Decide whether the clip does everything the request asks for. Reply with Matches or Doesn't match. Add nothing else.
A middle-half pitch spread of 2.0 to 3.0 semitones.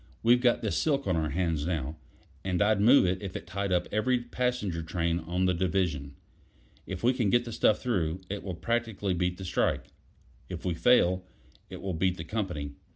Doesn't match